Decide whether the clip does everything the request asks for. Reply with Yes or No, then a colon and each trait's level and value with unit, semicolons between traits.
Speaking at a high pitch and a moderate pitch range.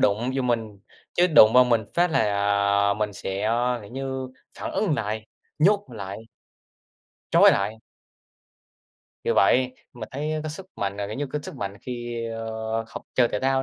No: low, 120 Hz; average, 3.8 semitones